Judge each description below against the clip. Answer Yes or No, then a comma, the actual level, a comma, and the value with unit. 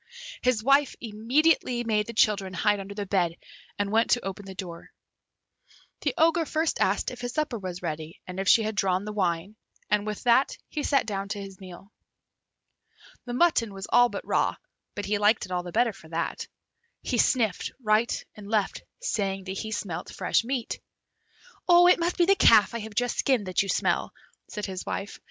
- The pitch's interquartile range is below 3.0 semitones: No, average, 3.9 semitones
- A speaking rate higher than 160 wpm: Yes, average, 195 wpm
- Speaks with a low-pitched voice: No, high, 210 Hz